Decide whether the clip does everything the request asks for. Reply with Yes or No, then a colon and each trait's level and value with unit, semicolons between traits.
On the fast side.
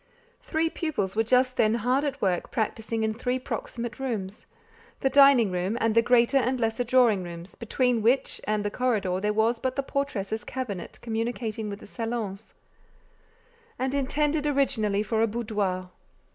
No: average, 160 wpm